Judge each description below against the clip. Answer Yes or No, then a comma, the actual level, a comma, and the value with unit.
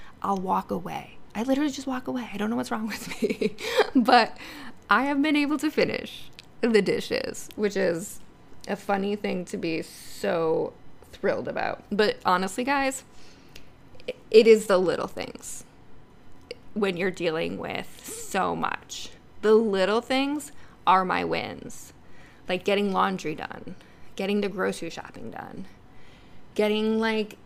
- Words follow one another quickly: No, average, 140 wpm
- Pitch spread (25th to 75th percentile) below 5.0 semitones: No, wide, 5.5 semitones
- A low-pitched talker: No, high, 215 Hz